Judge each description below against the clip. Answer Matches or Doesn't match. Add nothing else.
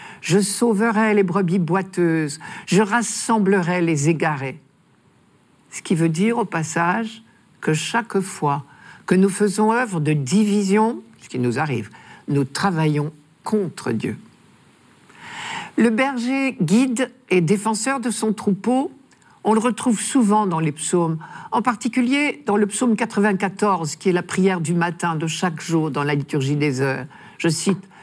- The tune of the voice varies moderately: Doesn't match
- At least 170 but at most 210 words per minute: Doesn't match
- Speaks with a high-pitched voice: Matches